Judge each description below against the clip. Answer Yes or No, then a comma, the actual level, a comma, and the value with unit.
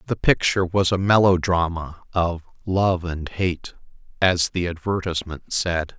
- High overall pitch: No, very low, 90 Hz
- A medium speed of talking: No, slow, 130 wpm